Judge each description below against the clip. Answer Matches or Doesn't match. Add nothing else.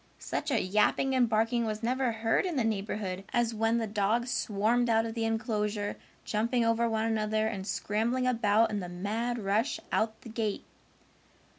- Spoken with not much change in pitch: Matches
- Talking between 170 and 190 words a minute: Matches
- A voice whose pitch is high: Matches